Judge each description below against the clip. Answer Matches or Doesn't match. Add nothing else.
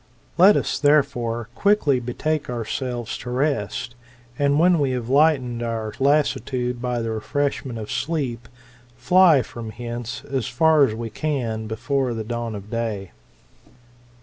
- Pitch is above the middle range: Doesn't match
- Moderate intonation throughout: Matches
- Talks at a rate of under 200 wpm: Matches